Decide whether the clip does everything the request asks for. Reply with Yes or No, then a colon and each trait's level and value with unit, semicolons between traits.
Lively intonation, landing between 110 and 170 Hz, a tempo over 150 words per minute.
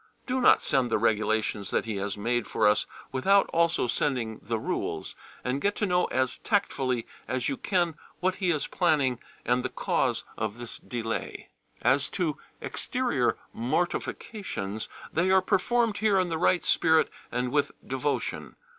Yes: wide, 7.4 semitones; low, 135 Hz; average, 160 wpm